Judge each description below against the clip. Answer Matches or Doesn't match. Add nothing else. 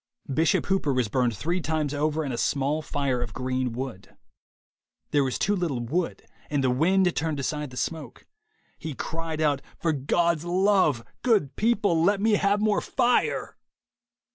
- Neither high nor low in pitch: Matches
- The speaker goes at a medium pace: Matches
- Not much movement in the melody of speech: Doesn't match